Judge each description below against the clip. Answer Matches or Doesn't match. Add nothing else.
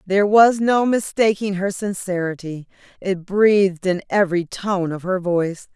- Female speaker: Matches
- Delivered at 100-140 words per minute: Matches